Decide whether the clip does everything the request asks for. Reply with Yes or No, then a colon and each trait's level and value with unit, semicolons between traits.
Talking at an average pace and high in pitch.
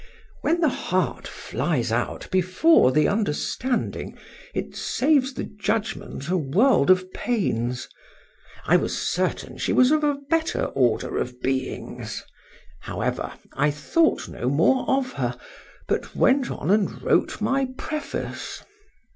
No: slow, 120 wpm; high, 205 Hz